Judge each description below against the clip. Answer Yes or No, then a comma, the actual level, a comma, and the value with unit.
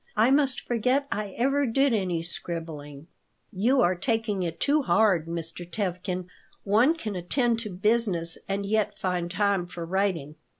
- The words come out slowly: No, average, 155 wpm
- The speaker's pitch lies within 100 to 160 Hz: No, high, 195 Hz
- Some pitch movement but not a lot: Yes, average, 4.9 semitones